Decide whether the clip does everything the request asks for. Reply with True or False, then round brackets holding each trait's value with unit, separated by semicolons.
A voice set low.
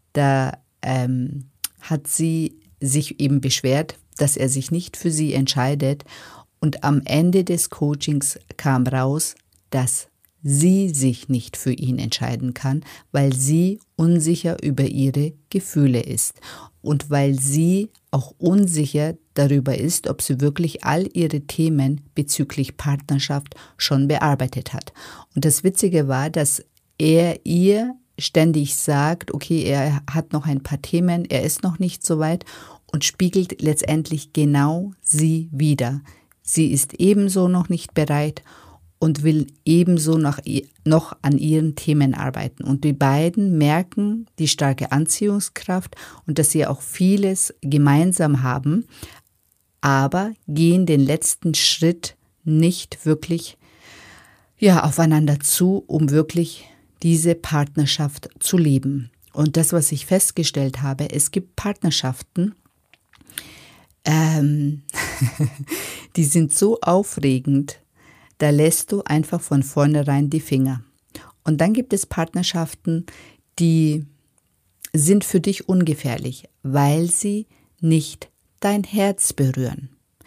False (150 Hz)